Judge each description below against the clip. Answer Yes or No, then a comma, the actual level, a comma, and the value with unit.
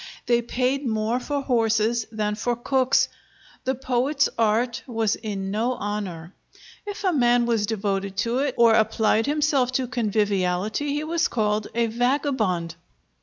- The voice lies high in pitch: Yes, high, 235 Hz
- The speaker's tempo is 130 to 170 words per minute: Yes, average, 145 wpm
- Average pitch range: Yes, average, 3.4 semitones